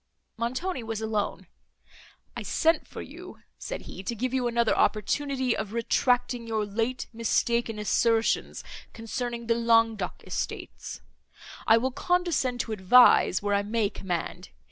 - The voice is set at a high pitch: Yes, high, 230 Hz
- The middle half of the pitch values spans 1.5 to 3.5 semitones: Yes, narrow, 2.4 semitones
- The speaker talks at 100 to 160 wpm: Yes, slow, 135 wpm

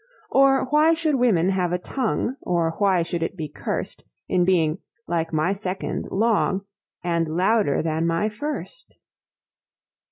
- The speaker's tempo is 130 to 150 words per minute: Yes, average, 140 wpm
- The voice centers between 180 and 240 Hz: Yes, medium, 185 Hz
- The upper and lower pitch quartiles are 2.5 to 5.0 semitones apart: No, wide, 5.6 semitones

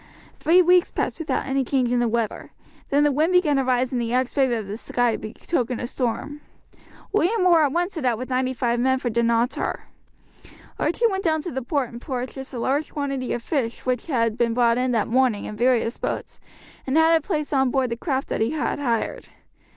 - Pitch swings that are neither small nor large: Yes, average, 3.7 semitones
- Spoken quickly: Yes, fast, 215 wpm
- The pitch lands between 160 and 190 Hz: No, very high, 260 Hz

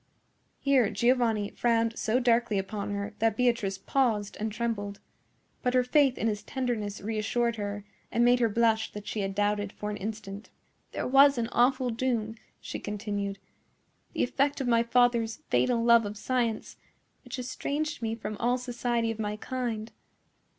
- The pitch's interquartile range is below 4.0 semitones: Yes, average, 2.8 semitones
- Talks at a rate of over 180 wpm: No, average, 165 wpm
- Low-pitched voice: No, high, 230 Hz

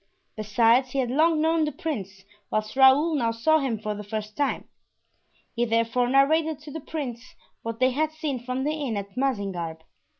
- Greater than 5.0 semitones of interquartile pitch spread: Yes, wide, 5.4 semitones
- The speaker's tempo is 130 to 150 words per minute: No, average, 180 wpm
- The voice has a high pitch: Yes, very high, 255 Hz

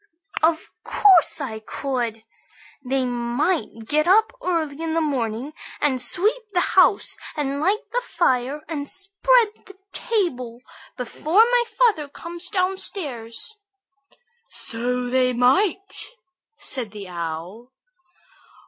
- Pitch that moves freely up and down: Yes, wide, 7.4 semitones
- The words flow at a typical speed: No, slow, 110 wpm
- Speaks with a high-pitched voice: Yes, very high, 295 Hz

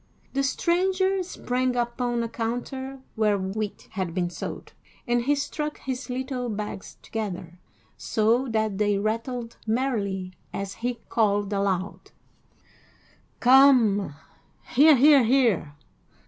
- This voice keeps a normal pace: No, slow, 115 wpm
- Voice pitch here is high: Yes, high, 235 Hz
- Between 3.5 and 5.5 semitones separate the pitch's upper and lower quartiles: Yes, average, 4.4 semitones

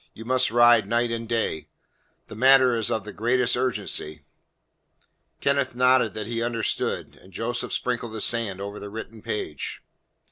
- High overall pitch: No, low, 115 Hz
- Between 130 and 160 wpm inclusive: Yes, average, 155 wpm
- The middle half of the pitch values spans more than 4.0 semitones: No, narrow, 2.4 semitones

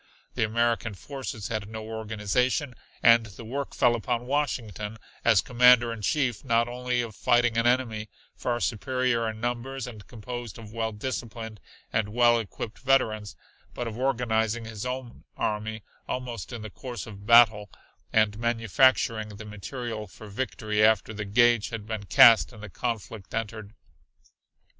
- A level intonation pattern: Yes, narrow, 2.2 semitones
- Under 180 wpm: Yes, average, 150 wpm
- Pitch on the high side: No, low, 115 Hz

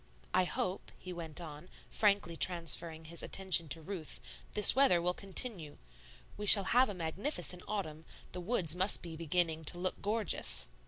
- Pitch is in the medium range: Yes, medium, 180 Hz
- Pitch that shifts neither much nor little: Yes, average, 3.4 semitones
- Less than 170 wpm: Yes, average, 160 wpm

